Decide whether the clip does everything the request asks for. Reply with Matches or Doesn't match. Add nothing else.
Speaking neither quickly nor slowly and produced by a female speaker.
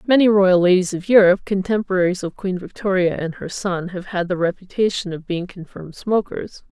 Matches